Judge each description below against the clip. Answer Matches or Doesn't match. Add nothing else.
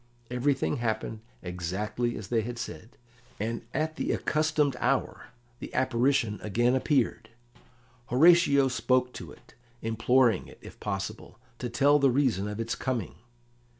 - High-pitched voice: Doesn't match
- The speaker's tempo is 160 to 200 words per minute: Doesn't match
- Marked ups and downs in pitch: Doesn't match